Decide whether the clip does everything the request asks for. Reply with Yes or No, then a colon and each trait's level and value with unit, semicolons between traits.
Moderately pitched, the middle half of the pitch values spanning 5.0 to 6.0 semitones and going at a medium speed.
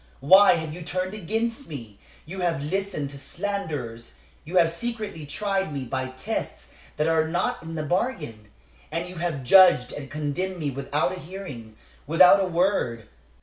Yes: medium, 165 Hz; average, 5.3 semitones; average, 165 wpm